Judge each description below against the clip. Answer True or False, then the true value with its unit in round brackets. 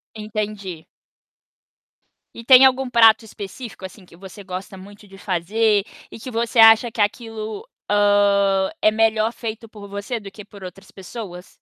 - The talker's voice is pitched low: False (210 Hz)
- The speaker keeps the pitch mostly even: True (2.3 semitones)